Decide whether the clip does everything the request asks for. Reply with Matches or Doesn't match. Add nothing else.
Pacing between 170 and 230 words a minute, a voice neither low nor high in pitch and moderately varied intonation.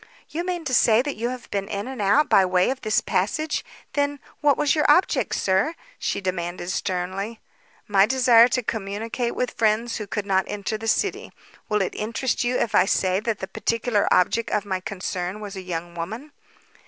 Doesn't match